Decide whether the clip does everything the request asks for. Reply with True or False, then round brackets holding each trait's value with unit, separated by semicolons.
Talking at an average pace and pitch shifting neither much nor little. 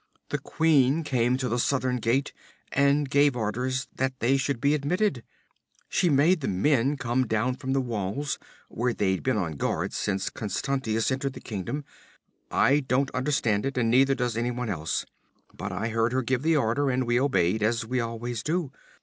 True (180 wpm; 3.3 semitones)